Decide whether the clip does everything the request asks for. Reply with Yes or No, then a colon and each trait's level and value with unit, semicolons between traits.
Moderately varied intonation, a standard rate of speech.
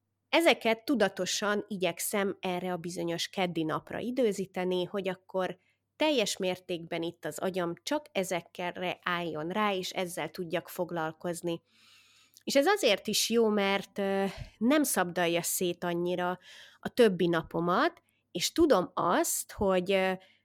Yes: average, 3.1 semitones; average, 120 wpm